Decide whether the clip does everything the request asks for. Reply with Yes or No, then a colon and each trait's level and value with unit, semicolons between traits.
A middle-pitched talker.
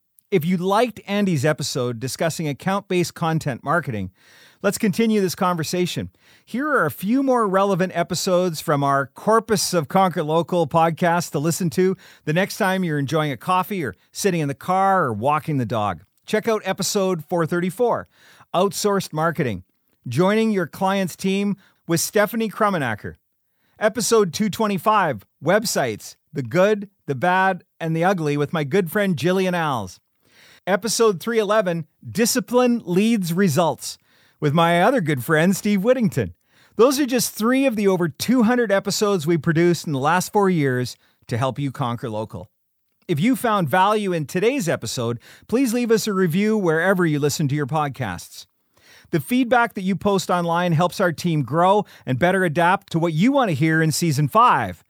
Yes: medium, 175 Hz